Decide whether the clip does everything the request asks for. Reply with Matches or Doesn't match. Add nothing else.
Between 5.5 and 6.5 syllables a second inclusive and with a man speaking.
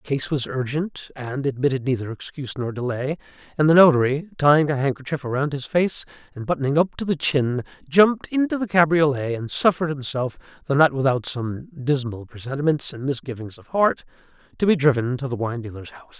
Matches